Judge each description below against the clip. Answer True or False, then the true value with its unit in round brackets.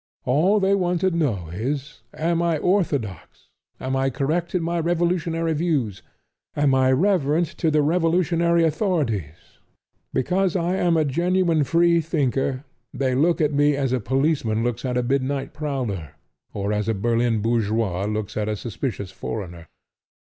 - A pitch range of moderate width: False (6.4 semitones)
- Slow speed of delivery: False (155 wpm)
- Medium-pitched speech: True (145 Hz)